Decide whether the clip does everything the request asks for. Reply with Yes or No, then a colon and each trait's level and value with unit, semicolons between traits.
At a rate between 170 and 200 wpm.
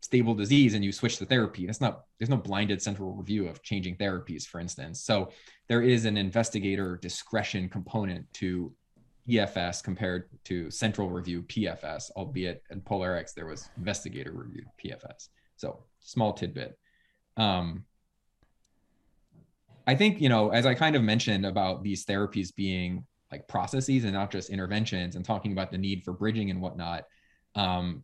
No: average, 160 wpm